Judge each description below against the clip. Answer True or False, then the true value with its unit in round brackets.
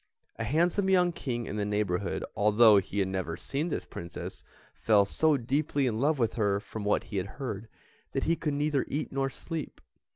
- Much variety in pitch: True (6.3 semitones)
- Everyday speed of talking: True (195 wpm)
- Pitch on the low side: True (120 Hz)